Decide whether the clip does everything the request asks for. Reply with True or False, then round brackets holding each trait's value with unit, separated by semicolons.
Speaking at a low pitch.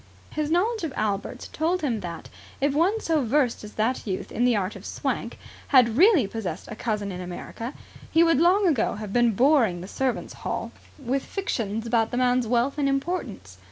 False (245 Hz)